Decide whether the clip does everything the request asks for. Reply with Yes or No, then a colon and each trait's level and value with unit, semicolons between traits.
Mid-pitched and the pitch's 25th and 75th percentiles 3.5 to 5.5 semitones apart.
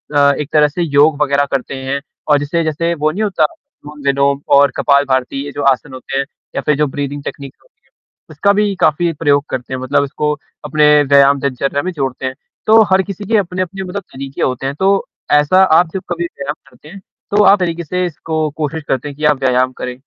Yes: medium, 150 Hz; average, 3.8 semitones